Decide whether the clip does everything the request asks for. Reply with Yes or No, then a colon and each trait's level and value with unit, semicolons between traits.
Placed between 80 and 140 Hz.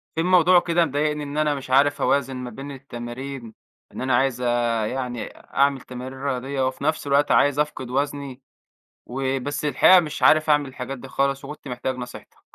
Yes: low, 135 Hz